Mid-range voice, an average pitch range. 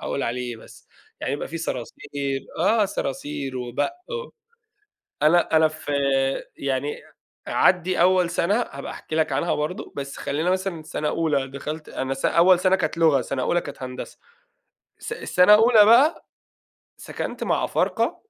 Yes: medium, 155 Hz; average, 4.7 semitones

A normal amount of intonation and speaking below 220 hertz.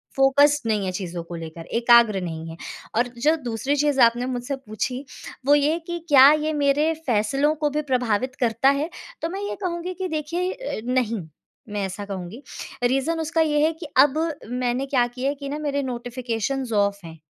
No: average, 4.9 semitones; very high, 260 Hz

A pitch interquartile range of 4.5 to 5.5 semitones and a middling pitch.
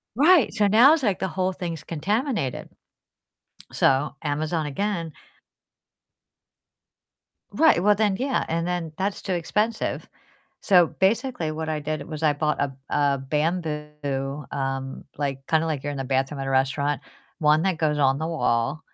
Yes: average, 4.9 semitones; medium, 155 Hz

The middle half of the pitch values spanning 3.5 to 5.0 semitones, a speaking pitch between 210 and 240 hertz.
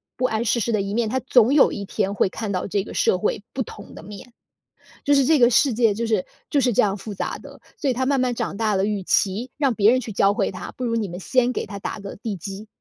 Yes: average, 3.8 semitones; high, 220 Hz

